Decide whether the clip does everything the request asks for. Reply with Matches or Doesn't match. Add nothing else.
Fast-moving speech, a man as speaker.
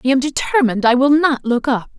Doesn't match